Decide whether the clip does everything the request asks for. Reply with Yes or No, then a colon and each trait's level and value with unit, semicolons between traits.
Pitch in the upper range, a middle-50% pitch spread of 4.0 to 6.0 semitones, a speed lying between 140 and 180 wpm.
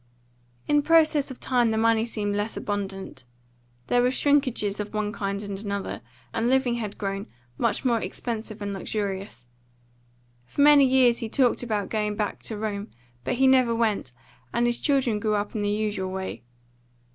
No: high, 220 Hz; average, 3.2 semitones; average, 170 wpm